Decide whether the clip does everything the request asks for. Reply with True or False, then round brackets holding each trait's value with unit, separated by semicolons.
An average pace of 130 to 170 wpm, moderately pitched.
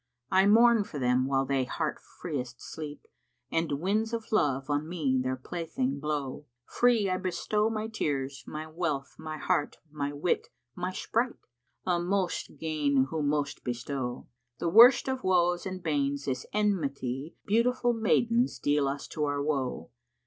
True (160 wpm; 155 Hz)